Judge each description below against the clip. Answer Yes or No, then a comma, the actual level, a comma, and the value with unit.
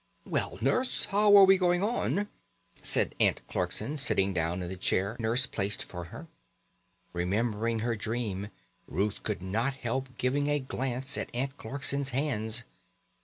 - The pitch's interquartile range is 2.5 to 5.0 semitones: No, wide, 5.5 semitones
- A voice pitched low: Yes, low, 120 Hz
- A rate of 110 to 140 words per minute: No, average, 155 wpm